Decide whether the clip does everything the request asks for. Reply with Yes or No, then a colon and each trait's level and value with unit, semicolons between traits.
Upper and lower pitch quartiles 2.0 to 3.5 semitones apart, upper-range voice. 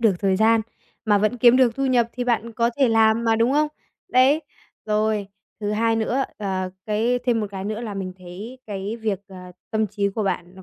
Yes: average, 2.8 semitones; high, 220 Hz